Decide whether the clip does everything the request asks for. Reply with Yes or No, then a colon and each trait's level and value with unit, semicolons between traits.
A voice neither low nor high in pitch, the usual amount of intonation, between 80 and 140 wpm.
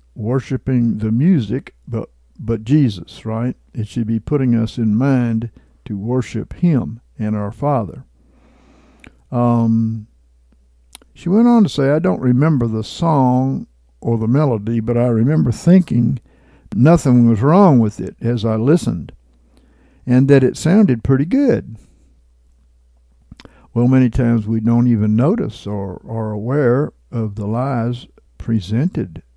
No: low, 115 Hz; average, 3.5 semitones; slow, 135 wpm